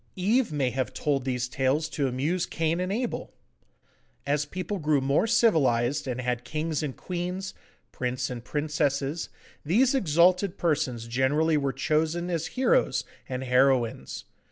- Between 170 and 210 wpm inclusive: No, average, 140 wpm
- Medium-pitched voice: Yes, medium, 150 Hz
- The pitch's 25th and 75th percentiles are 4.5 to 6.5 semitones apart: Yes, average, 5.1 semitones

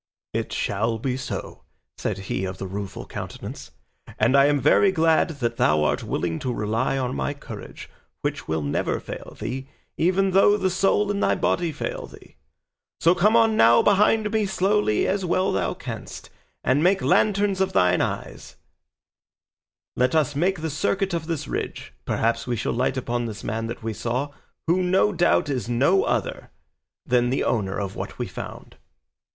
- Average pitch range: No, wide, 8.7 semitones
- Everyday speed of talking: Yes, average, 180 wpm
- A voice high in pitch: No, low, 135 Hz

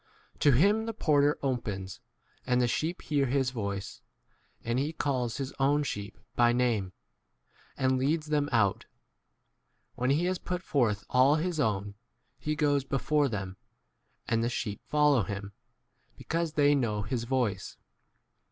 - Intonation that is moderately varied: Yes, average, 4.6 semitones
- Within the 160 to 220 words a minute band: No, average, 150 wpm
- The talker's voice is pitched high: No, low, 130 Hz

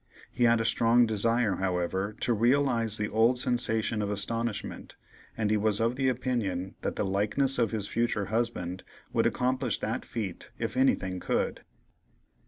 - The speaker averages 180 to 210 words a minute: No, average, 160 wpm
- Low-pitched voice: Yes, low, 115 Hz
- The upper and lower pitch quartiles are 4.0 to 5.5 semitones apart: No, average, 3.0 semitones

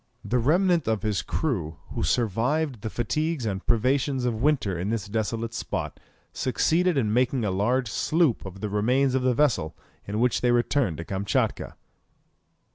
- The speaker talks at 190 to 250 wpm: No, average, 165 wpm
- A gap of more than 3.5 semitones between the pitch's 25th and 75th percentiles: Yes, average, 4.6 semitones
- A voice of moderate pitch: No, low, 120 Hz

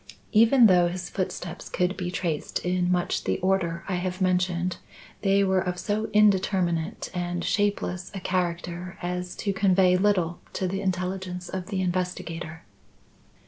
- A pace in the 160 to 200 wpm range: No, average, 145 wpm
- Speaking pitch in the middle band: Yes, medium, 180 Hz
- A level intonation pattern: Yes, narrow, 1.4 semitones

